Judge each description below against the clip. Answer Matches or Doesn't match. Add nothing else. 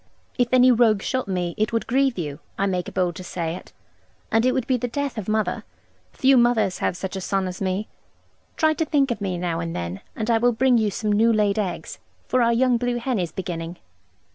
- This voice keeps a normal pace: Doesn't match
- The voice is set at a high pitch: Matches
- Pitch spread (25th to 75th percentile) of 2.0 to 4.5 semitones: Doesn't match